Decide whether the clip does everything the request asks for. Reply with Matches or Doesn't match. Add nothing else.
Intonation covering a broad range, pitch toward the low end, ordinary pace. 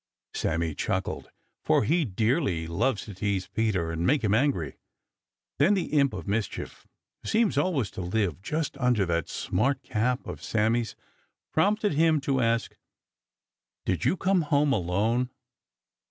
Matches